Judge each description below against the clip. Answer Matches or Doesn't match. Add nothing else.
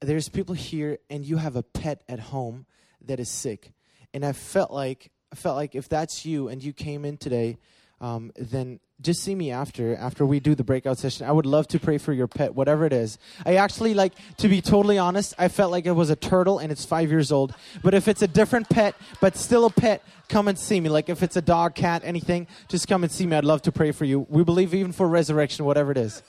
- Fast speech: Matches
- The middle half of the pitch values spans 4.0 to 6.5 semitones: Matches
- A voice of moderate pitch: Matches